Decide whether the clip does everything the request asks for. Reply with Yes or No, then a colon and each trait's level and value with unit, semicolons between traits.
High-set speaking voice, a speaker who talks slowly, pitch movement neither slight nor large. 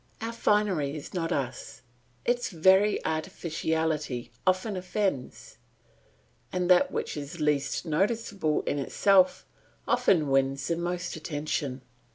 No: medium, 165 Hz; slow, 115 wpm; average, 4.4 semitones